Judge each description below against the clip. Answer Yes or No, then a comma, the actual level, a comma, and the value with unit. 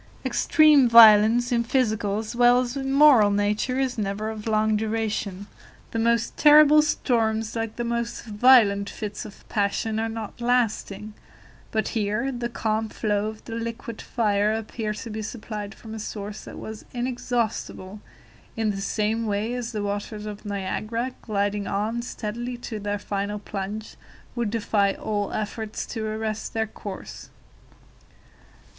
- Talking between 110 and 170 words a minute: Yes, average, 150 wpm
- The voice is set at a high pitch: Yes, high, 220 Hz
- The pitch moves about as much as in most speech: No, narrow, 2.2 semitones